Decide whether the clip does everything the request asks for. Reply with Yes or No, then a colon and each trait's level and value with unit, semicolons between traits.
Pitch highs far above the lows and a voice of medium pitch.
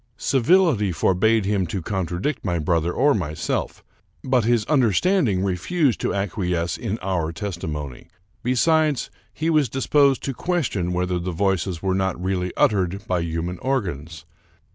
No: wide, 6.5 semitones; very low, 95 Hz